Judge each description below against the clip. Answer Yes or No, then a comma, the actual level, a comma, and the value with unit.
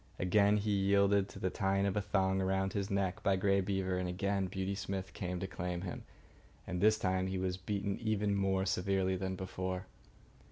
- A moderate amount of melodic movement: No, narrow, 1.2 semitones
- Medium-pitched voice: No, very low, 95 Hz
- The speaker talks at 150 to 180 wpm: No, average, 195 wpm